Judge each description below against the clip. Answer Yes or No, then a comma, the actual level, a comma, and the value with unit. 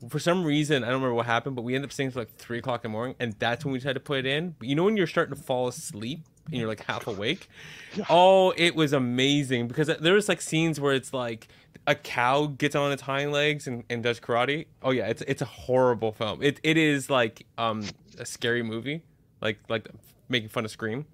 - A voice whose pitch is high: No, low, 135 Hz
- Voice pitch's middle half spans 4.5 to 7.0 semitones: No, average, 3.8 semitones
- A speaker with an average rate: No, fast, 245 wpm